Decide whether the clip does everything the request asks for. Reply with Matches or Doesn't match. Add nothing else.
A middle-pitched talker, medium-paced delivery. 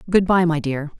Doesn't match